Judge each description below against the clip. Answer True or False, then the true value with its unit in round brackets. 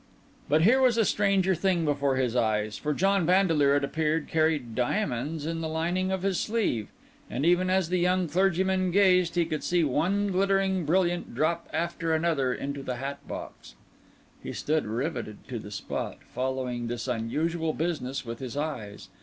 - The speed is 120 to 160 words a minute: False (170 wpm)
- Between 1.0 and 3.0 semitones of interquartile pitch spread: False (5.6 semitones)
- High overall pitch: False (160 Hz)